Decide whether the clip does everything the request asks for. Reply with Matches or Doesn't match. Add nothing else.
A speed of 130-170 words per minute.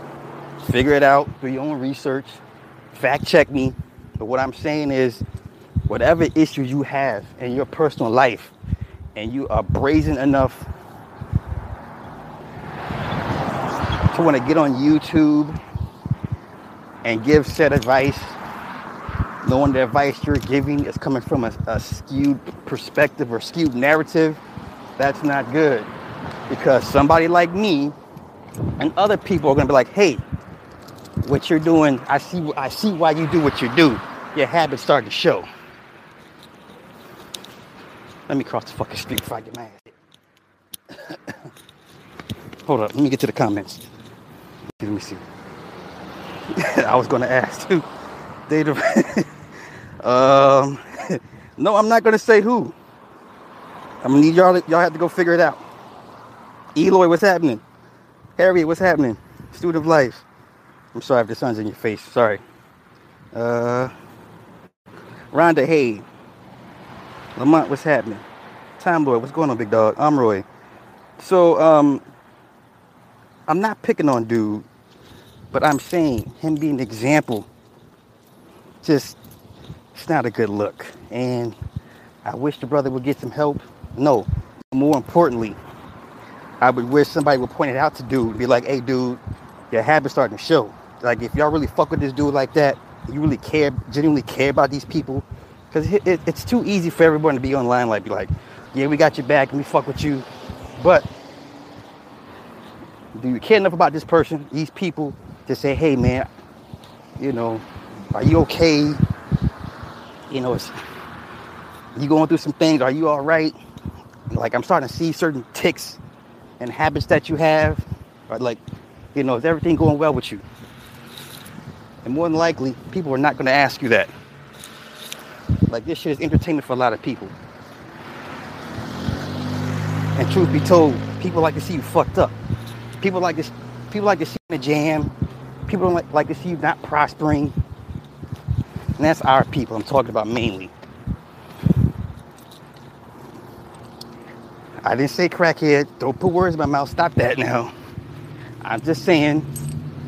Matches